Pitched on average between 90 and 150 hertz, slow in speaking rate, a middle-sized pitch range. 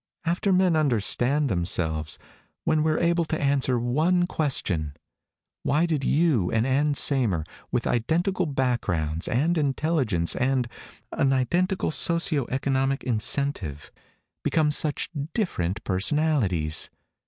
No: low, 135 Hz; slow, 110 wpm; wide, 6.3 semitones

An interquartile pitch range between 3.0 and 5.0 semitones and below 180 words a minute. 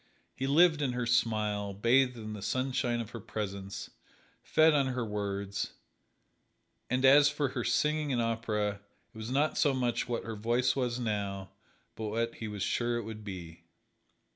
Yes: average, 3.7 semitones; average, 170 wpm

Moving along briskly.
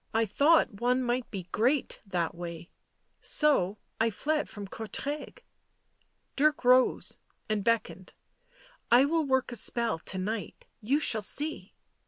No: average, 150 wpm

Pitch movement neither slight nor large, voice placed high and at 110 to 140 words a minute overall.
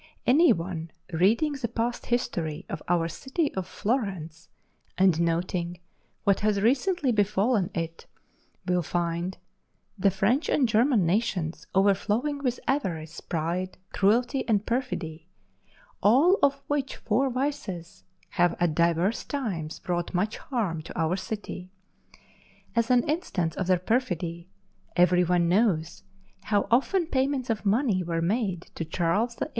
No: wide, 6.1 semitones; high, 195 Hz; slow, 135 wpm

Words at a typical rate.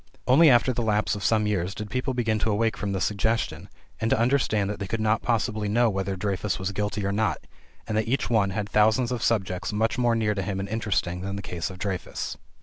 No: fast, 240 wpm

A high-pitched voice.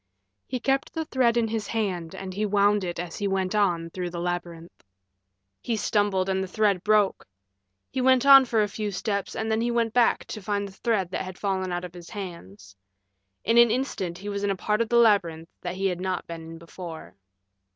Yes: high, 200 Hz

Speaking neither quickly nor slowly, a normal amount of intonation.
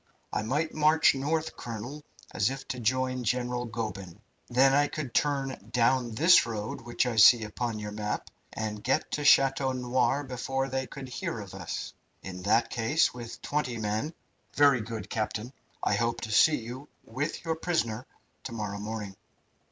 Yes: average, 170 wpm; average, 3.7 semitones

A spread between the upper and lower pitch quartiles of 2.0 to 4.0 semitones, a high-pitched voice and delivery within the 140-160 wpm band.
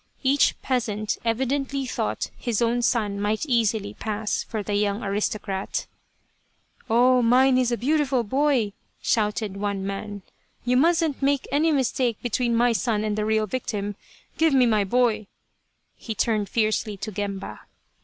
Yes: average, 3.6 semitones; high, 230 Hz; average, 155 wpm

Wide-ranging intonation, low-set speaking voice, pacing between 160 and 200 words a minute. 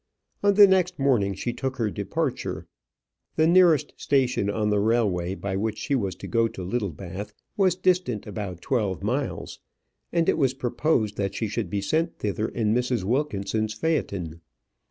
Yes: wide, 5.9 semitones; low, 115 Hz; average, 165 wpm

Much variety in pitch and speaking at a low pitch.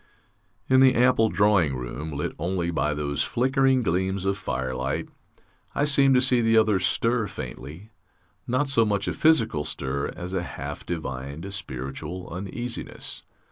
Yes: wide, 8.3 semitones; very low, 95 Hz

